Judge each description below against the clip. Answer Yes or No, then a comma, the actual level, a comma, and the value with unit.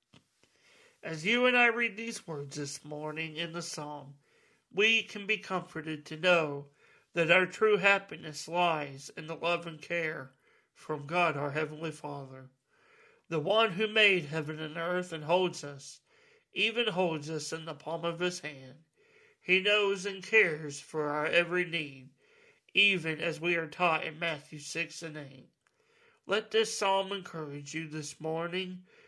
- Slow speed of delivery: No, average, 160 wpm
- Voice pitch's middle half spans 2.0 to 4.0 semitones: No, average, 4.6 semitones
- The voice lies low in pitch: No, medium, 170 Hz